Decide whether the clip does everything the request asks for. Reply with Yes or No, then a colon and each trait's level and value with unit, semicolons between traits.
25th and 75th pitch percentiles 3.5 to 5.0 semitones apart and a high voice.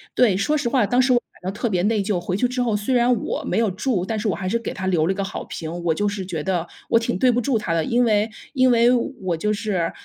Yes: average, 4.5 semitones; high, 210 Hz